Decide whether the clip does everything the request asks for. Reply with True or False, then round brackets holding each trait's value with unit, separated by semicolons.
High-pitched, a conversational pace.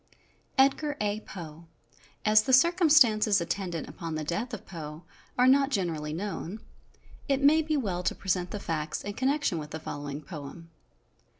True (195 Hz; 160 wpm)